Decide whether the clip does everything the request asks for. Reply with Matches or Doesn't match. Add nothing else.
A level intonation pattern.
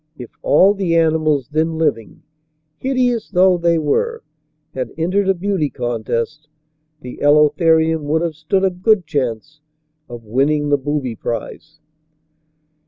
Doesn't match